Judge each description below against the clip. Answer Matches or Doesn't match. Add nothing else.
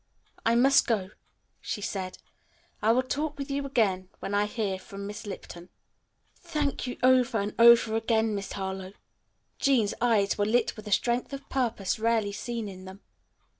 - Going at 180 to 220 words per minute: Doesn't match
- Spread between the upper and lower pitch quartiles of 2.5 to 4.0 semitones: Matches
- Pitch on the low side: Doesn't match